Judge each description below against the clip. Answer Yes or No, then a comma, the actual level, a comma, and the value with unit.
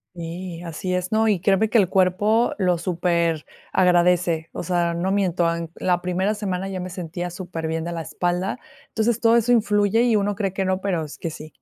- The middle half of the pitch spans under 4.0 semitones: Yes, average, 2.8 semitones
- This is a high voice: No, medium, 180 Hz